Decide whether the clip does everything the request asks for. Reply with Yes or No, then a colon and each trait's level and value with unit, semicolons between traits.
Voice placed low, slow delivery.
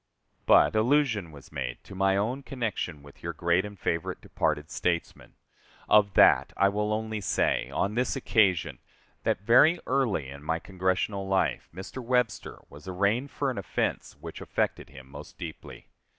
No: low, 100 Hz; average, 160 wpm